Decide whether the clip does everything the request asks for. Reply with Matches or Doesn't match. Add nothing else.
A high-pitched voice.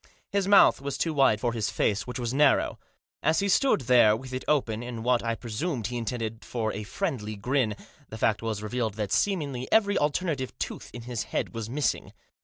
Doesn't match